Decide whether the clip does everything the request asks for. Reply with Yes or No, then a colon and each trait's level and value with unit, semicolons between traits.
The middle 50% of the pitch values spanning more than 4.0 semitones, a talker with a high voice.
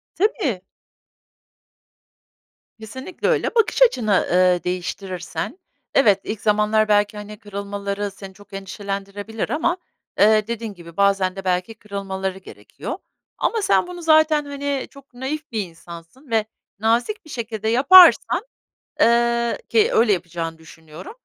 Yes: wide, 5.4 semitones; high, 210 Hz